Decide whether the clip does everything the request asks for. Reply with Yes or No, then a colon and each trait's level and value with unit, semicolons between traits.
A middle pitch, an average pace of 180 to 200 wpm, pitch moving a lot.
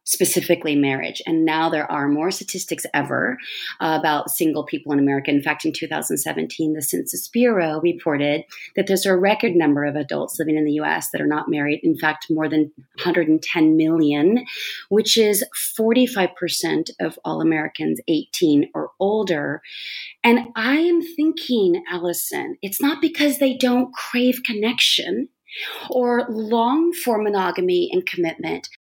No: medium, 180 Hz; average, 150 wpm; wide, 8.1 semitones